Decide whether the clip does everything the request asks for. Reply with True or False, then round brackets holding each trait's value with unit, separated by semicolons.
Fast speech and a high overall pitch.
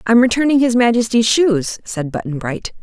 False (170 wpm; 225 Hz)